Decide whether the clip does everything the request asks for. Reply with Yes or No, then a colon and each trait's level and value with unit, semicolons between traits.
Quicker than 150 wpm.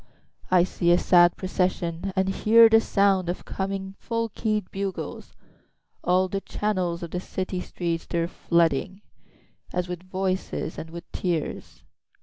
No: slow, 135 wpm